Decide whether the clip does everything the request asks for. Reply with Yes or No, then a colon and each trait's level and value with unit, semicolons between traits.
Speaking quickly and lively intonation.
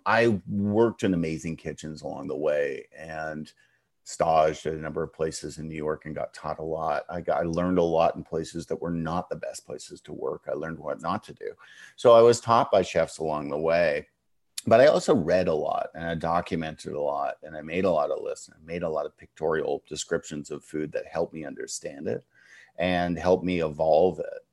Yes: fast, 225 wpm; wide, 6.7 semitones